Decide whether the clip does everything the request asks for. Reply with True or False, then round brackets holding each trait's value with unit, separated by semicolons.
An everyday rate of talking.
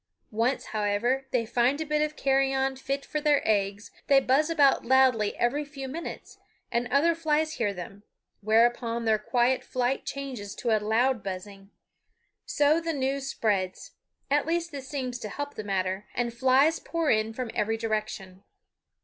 True (165 wpm)